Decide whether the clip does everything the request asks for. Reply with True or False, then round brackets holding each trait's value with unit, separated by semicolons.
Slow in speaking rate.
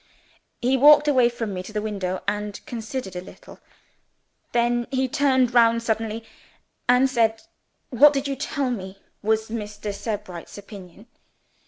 False (145 wpm)